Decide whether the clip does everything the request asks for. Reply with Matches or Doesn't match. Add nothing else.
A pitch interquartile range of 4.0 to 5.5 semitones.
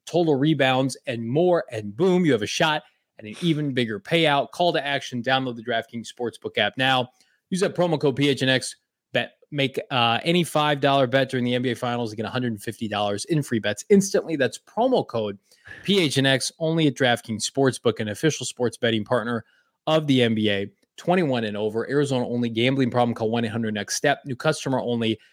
Matches